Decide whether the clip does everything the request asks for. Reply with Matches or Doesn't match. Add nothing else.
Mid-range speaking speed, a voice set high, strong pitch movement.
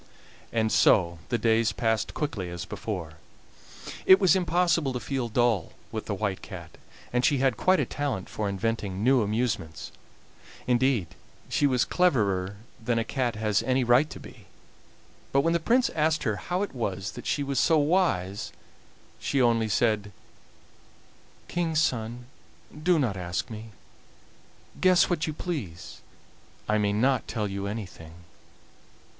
Doesn't match